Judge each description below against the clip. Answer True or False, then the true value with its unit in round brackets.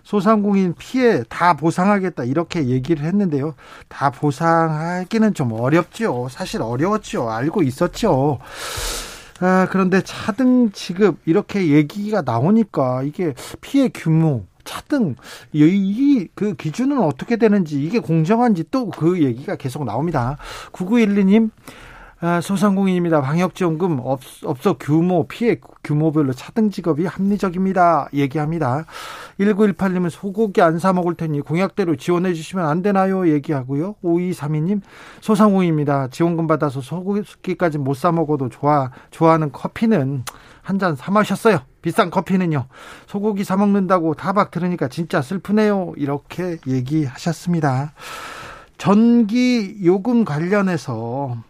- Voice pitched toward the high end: False (175 Hz)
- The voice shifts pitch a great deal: False (4.9 semitones)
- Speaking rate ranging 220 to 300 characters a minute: True (290 characters per minute)